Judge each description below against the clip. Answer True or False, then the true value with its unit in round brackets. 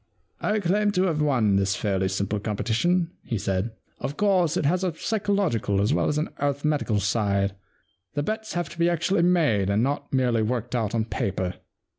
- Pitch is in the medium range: False (130 Hz)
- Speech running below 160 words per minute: False (195 wpm)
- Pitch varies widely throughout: True (9.0 semitones)